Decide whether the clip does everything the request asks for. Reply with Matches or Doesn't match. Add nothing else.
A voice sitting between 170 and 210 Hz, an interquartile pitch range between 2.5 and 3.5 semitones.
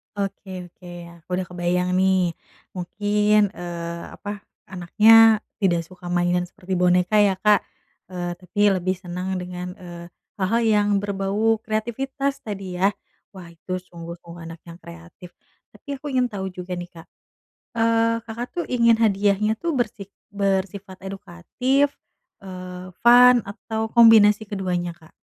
Matches